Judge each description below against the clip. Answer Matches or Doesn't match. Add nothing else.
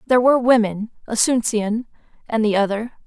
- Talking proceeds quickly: Doesn't match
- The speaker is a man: Doesn't match